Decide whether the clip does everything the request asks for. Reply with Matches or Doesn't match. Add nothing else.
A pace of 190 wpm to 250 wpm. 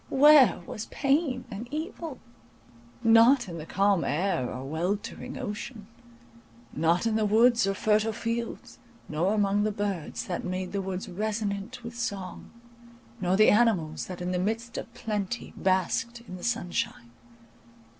Doesn't match